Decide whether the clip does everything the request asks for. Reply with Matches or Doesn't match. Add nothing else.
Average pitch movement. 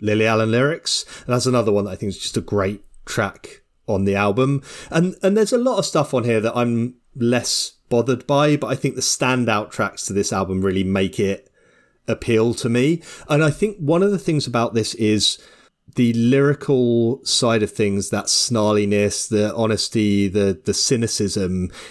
Matches